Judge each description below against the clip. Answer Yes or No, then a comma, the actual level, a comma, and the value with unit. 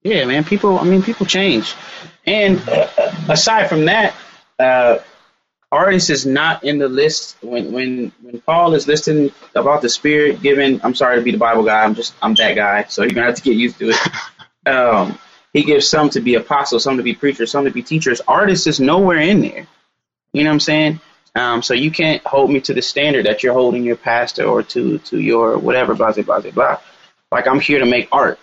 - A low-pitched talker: No, medium, 145 Hz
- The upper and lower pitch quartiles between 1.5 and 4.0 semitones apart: No, average, 4.4 semitones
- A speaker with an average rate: No, fast, 215 wpm